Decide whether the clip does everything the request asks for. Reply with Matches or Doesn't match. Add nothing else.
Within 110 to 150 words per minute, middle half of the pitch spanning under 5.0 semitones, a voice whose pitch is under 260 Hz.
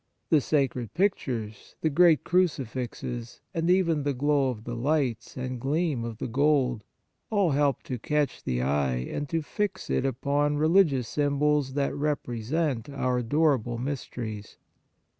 Matches